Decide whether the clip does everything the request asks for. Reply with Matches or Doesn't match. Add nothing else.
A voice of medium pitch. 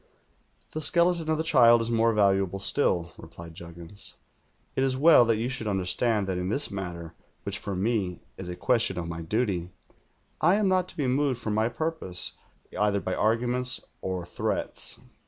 Doesn't match